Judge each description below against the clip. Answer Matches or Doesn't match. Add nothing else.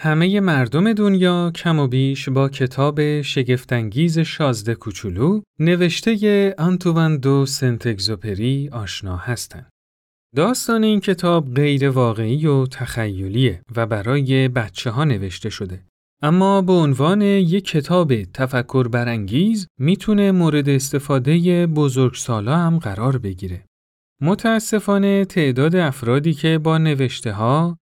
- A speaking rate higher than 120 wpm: Doesn't match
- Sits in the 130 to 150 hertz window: Matches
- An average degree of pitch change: Doesn't match